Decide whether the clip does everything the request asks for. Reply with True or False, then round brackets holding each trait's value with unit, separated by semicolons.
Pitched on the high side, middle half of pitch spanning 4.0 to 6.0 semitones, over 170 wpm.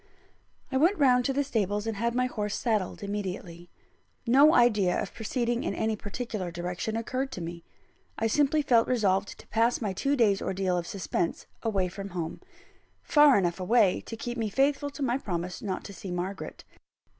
True (215 Hz; 4.9 semitones; 180 wpm)